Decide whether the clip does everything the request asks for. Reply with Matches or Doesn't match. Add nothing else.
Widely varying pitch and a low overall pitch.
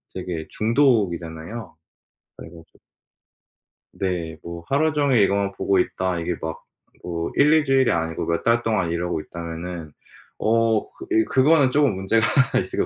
Matches